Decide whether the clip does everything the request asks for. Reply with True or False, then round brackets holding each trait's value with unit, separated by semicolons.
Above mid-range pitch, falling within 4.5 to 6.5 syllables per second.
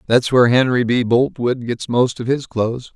False (120 Hz; 5.1 syllables/s)